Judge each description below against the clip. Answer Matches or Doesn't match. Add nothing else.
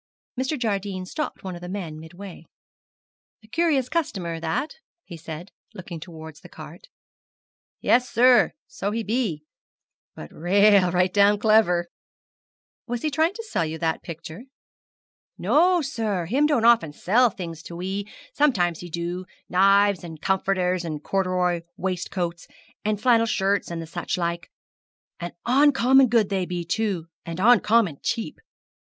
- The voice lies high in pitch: Matches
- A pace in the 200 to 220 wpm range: Doesn't match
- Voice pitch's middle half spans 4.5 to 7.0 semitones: Matches